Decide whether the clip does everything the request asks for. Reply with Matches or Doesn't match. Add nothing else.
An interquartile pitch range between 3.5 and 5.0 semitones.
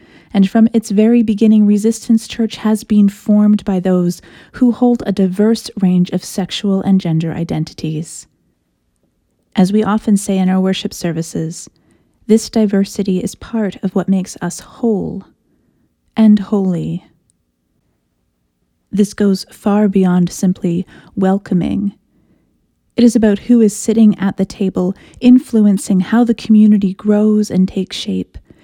Doesn't match